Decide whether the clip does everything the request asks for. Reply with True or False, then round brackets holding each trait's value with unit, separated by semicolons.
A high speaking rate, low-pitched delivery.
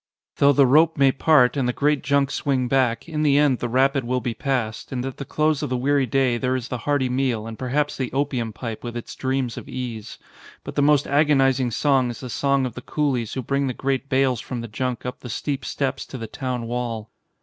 True (240 wpm; 130 Hz)